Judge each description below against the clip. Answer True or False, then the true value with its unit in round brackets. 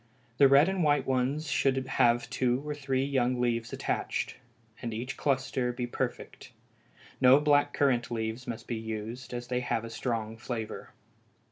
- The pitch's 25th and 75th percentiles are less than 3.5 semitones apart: True (2.5 semitones)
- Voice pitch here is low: True (125 Hz)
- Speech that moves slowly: False (160 wpm)